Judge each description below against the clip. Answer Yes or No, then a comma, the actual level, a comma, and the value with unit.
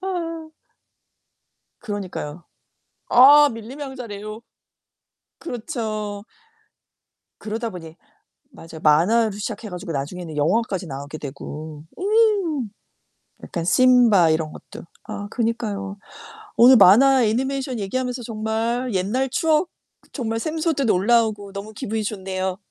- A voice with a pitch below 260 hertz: Yes, high, 220 Hz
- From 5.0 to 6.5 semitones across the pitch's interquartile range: Yes, average, 5.3 semitones